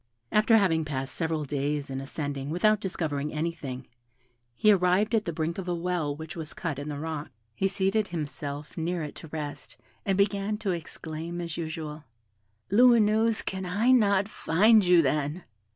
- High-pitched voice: No, medium, 165 Hz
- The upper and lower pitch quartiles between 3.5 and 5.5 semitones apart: Yes, average, 4.8 semitones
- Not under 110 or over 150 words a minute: No, average, 170 wpm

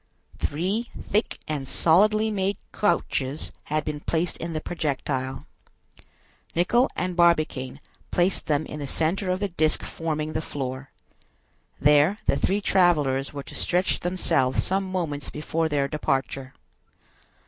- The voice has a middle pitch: Yes, medium, 155 Hz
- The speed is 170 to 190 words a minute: No, slow, 135 wpm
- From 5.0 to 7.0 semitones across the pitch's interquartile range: No, average, 4.2 semitones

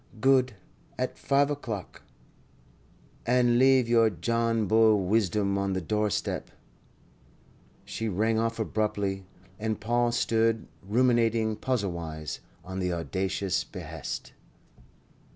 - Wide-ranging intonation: No, average, 3.3 semitones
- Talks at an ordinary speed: No, slow, 100 wpm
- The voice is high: No, low, 110 Hz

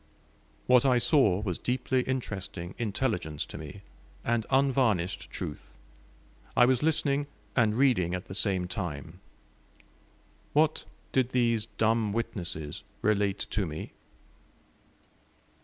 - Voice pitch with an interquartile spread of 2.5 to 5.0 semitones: No, wide, 5.5 semitones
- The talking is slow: Yes, slow, 110 wpm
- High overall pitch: No, low, 110 Hz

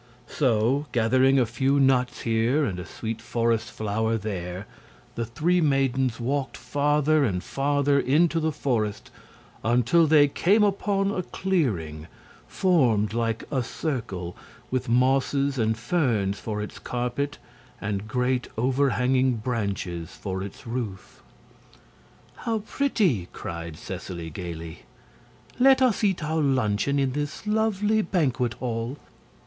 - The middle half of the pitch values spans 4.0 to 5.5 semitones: Yes, average, 5.1 semitones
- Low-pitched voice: Yes, low, 125 Hz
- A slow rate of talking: Yes, slow, 125 wpm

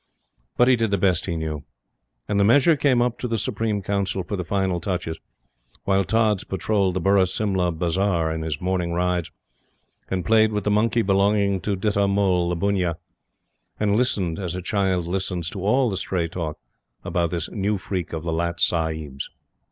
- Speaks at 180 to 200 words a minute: Yes, average, 185 wpm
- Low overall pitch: Yes, very low, 95 Hz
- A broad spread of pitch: No, average, 3.1 semitones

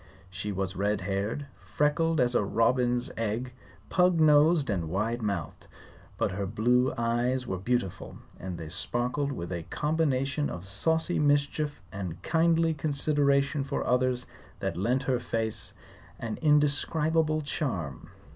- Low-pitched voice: Yes, low, 125 Hz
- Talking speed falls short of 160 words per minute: Yes, slow, 135 wpm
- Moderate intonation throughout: No, wide, 6.6 semitones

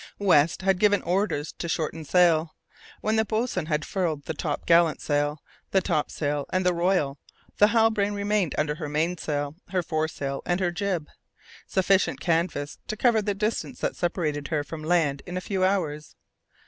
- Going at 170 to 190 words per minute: Yes, average, 175 wpm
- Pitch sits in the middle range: Yes, medium, 170 Hz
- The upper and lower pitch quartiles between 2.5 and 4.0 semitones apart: No, average, 4.4 semitones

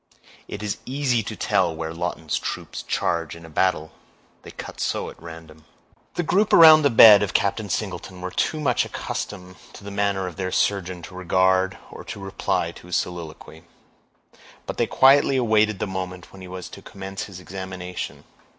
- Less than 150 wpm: No, average, 180 wpm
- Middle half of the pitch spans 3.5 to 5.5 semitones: No, average, 2.8 semitones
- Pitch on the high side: No, very low, 95 Hz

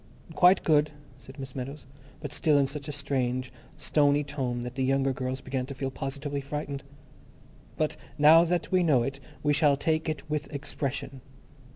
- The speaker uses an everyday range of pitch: No, narrow, 2.0 semitones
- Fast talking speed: No, average, 175 wpm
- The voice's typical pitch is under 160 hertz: Yes, medium, 140 Hz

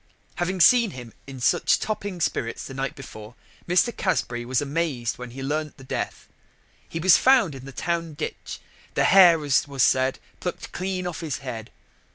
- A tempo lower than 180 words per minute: No, average, 185 wpm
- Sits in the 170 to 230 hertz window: No, medium, 145 Hz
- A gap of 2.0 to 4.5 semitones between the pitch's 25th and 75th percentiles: No, wide, 5.5 semitones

